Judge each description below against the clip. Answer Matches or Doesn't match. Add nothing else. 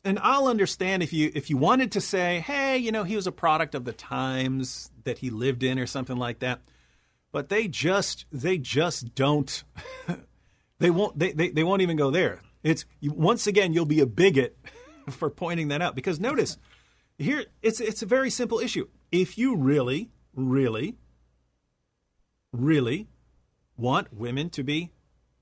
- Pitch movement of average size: Doesn't match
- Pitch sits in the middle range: Matches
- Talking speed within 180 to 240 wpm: Doesn't match